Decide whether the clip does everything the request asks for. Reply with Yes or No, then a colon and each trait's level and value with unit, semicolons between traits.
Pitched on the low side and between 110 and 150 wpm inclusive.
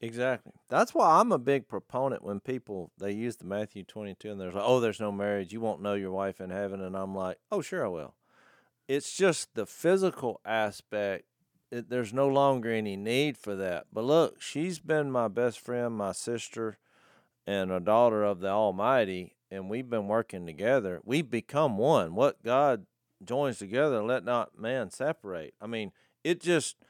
No: low, 110 Hz; average, 185 wpm